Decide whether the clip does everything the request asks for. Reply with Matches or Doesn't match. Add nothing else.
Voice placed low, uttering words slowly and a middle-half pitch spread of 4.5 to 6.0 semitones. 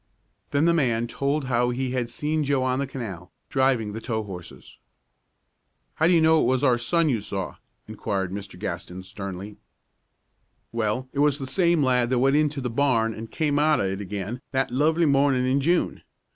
Doesn't match